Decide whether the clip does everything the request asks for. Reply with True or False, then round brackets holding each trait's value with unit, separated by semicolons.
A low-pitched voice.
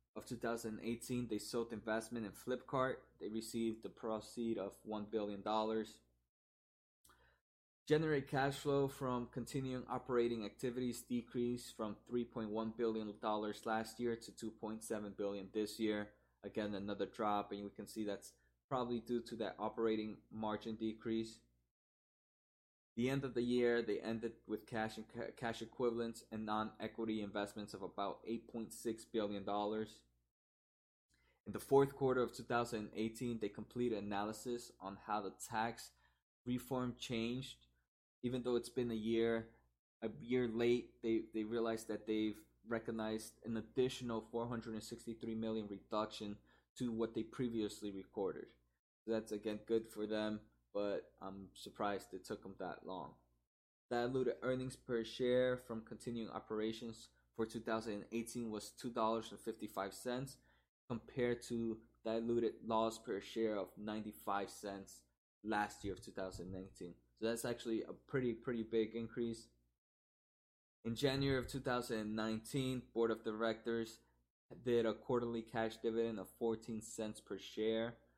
True (110 Hz)